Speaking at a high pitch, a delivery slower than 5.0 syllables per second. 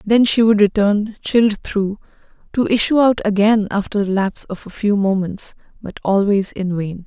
Yes: high, 205 Hz; 4.8 syllables/s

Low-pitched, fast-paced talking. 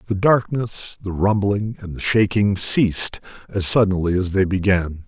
No: low, 100 Hz; average, 155 wpm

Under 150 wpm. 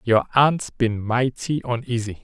Yes: slow, 135 wpm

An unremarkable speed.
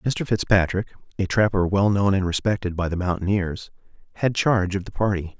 Yes: average, 180 wpm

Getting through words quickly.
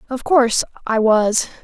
No: average, 145 wpm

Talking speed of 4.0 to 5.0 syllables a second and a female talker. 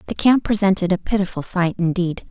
No: 5.8 syllables/s; female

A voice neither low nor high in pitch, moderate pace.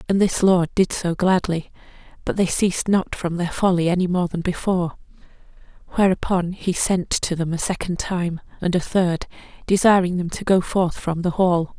Yes: medium, 180 Hz; average, 185 wpm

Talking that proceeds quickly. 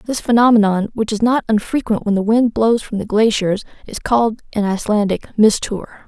No: average, 180 wpm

